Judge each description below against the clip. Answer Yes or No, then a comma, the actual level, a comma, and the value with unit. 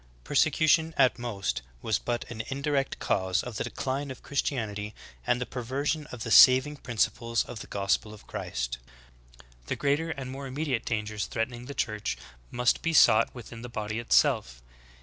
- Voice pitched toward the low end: Yes, low, 120 Hz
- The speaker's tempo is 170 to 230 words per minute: Yes, average, 180 wpm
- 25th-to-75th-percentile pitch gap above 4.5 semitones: No, average, 4.2 semitones